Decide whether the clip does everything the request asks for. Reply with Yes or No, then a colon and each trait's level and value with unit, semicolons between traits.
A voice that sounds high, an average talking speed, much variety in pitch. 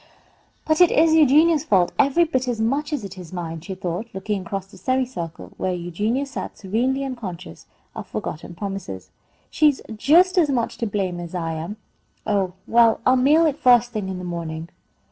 Yes: high, 215 Hz; average, 185 wpm; wide, 7.2 semitones